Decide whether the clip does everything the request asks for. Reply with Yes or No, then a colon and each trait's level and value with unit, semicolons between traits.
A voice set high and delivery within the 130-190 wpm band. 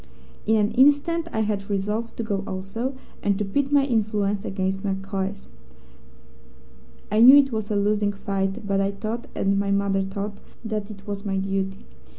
Yes: high, 205 Hz; average, 170 wpm